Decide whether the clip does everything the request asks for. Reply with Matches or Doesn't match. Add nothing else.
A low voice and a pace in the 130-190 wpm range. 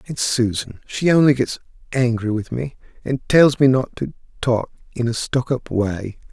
Matches